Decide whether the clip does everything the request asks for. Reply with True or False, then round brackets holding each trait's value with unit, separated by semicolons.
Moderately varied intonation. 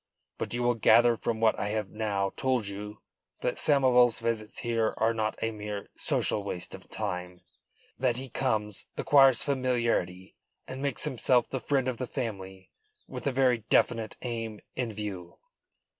True (3.2 semitones)